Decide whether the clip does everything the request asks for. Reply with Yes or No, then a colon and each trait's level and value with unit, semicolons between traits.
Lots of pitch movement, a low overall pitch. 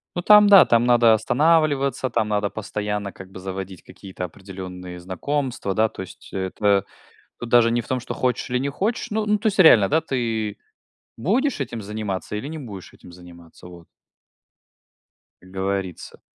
Yes: wide, 6.4 semitones; low, 110 Hz